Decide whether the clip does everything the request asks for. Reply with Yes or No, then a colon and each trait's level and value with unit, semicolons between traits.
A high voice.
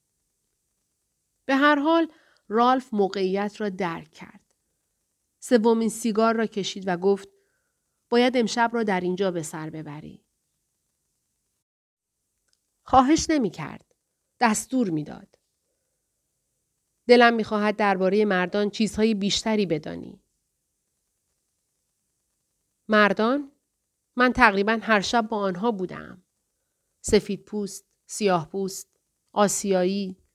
Yes: high, 210 Hz